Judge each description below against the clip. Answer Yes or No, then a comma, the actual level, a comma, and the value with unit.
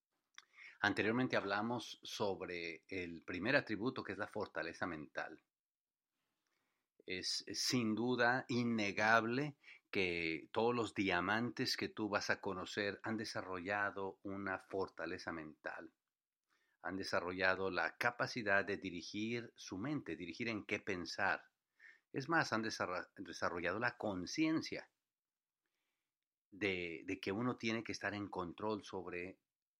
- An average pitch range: Yes, average, 3.4 semitones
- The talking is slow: Yes, slow, 120 wpm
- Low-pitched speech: Yes, low, 100 Hz